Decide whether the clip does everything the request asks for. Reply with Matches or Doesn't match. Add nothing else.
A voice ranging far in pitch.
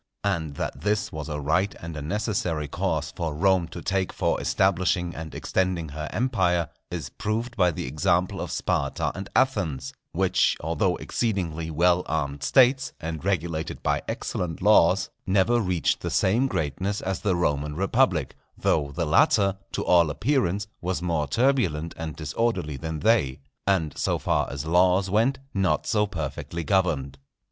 Doesn't match